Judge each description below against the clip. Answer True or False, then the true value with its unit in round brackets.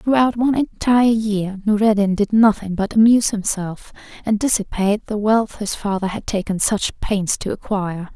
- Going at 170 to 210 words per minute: False (160 wpm)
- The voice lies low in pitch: False (210 Hz)